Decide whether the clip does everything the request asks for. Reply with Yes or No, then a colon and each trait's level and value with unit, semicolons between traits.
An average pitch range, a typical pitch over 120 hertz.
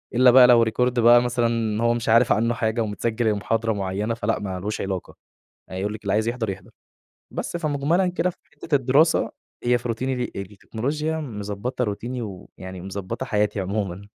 No: average, 3.3 semitones; low, 115 Hz